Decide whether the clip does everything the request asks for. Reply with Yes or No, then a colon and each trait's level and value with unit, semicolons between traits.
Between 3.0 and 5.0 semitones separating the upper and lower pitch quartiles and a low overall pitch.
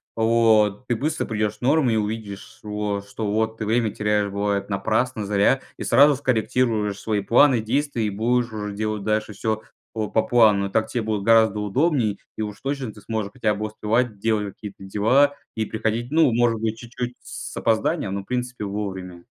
No: narrow, 2.4 semitones; low, 110 Hz